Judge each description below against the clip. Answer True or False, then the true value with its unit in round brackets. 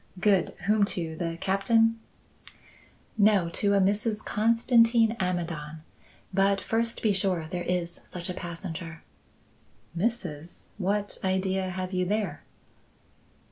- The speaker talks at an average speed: False (115 wpm)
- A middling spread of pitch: True (3.3 semitones)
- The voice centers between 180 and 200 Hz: True (190 Hz)